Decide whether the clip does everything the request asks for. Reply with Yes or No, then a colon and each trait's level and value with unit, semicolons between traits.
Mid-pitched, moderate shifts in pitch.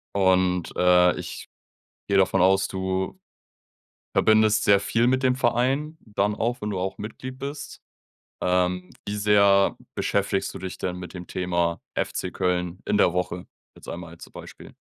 No: very low, 95 Hz; average, 3.1 semitones